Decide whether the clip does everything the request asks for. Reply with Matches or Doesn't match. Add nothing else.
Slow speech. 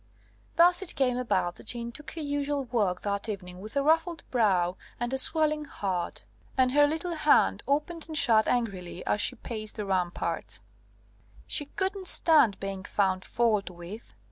Doesn't match